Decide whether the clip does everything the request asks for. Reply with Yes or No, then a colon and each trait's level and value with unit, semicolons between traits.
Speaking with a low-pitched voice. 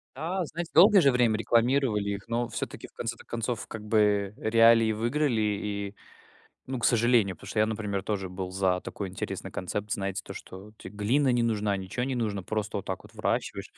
Yes: low, 110 Hz